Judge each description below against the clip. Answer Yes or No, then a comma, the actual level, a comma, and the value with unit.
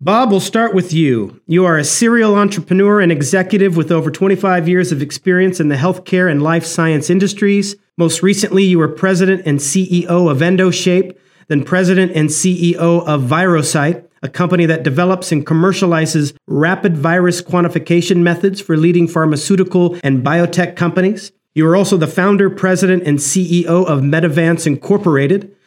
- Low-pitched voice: No, medium, 175 Hz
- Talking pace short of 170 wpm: Yes, average, 155 wpm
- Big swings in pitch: No, average, 2.8 semitones